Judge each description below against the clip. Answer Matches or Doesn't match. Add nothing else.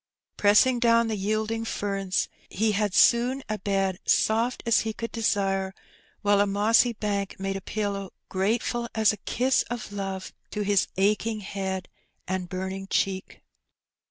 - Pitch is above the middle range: Matches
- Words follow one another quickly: Doesn't match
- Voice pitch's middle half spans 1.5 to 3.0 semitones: Matches